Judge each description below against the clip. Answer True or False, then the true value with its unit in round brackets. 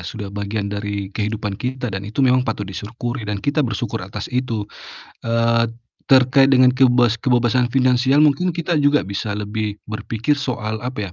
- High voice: False (115 Hz)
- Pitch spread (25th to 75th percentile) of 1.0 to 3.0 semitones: False (3.6 semitones)